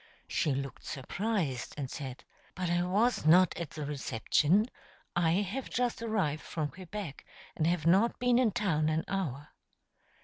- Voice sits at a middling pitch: Yes, medium, 175 Hz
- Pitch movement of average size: No, wide, 5.7 semitones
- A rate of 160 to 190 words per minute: No, average, 150 wpm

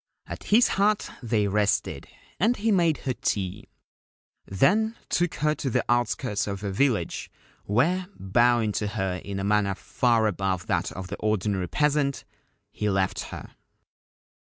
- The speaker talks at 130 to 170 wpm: Yes, average, 150 wpm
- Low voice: Yes, low, 110 Hz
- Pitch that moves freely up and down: Yes, wide, 6.9 semitones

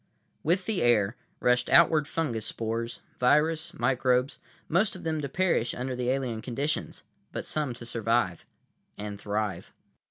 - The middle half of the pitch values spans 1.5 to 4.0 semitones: No, average, 5.1 semitones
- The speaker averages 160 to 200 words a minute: No, slow, 135 wpm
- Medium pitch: No, low, 125 Hz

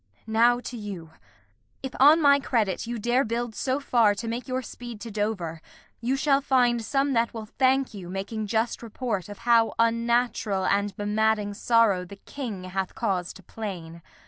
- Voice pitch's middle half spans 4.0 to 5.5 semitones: No, average, 3.3 semitones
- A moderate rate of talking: Yes, average, 170 wpm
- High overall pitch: Yes, high, 225 Hz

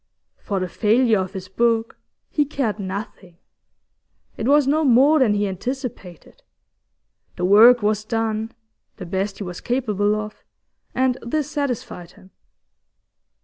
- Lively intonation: No, average, 4.6 semitones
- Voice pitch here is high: Yes, high, 220 Hz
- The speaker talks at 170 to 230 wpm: No, slow, 135 wpm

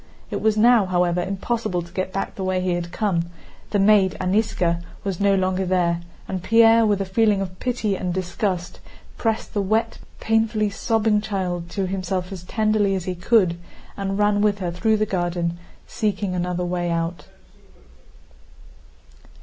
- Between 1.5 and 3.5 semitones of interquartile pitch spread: Yes, average, 2.9 semitones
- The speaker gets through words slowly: No, average, 165 wpm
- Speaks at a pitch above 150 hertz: Yes, high, 190 Hz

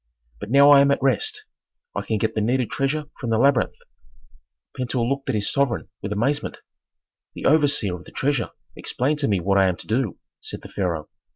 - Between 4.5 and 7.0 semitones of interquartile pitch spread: Yes, average, 5.1 semitones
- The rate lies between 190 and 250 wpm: Yes, average, 200 wpm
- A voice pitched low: Yes, low, 125 Hz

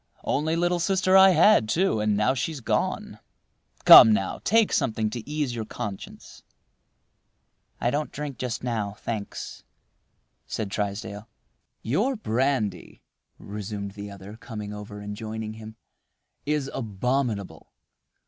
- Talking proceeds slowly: Yes, slow, 125 wpm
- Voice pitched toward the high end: No, low, 110 Hz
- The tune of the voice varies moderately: No, wide, 5.7 semitones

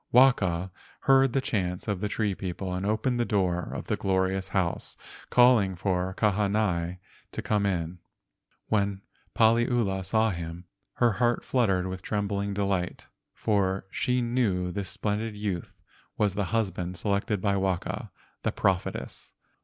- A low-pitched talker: Yes, low, 100 Hz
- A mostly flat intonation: No, average, 3.0 semitones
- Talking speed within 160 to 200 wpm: No, average, 140 wpm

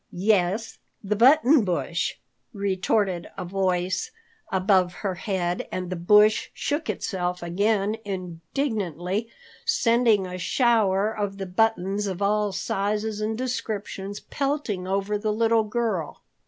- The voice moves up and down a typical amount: Yes, average, 3.2 semitones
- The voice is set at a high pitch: Yes, high, 200 Hz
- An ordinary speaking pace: No, slow, 120 wpm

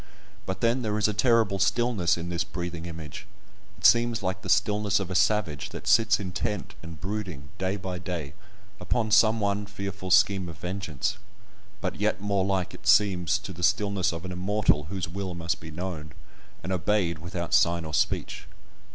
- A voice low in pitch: Yes, very low, 95 Hz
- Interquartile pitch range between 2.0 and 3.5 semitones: Yes, average, 3.0 semitones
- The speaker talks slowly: No, average, 180 wpm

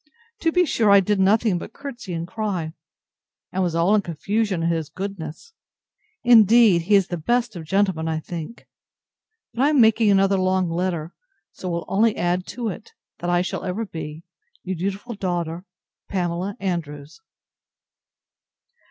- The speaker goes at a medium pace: Yes, average, 160 wpm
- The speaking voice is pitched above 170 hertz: Yes, high, 190 Hz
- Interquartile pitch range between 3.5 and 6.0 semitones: Yes, average, 3.9 semitones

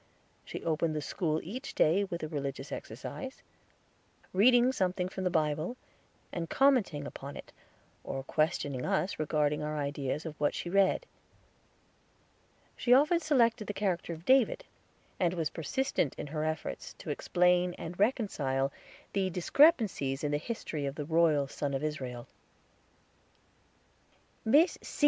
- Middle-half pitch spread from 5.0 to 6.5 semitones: Yes, wide, 5.6 semitones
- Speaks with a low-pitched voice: No, medium, 170 Hz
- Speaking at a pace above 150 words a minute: No, average, 140 wpm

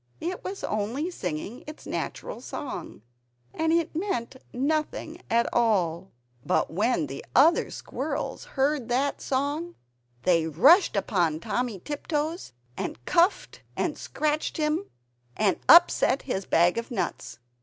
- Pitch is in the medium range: No, very high, 265 Hz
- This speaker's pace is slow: Yes, slow, 125 wpm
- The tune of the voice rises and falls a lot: Yes, wide, 8.1 semitones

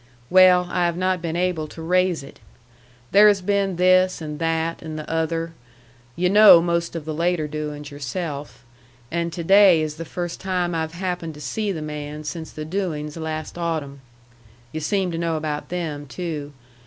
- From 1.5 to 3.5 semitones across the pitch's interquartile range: Yes, average, 2.8 semitones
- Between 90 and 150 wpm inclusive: No, average, 180 wpm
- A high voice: No, medium, 165 Hz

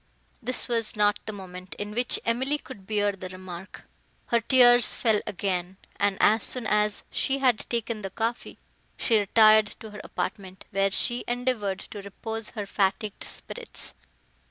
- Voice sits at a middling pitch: No, high, 210 Hz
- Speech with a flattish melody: No, average, 3.2 semitones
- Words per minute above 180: No, average, 155 wpm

